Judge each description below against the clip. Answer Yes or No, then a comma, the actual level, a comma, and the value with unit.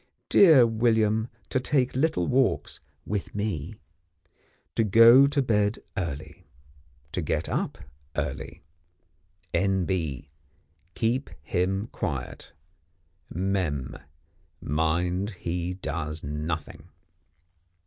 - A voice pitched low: Yes, very low, 95 Hz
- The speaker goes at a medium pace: No, slow, 85 wpm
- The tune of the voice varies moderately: No, wide, 5.9 semitones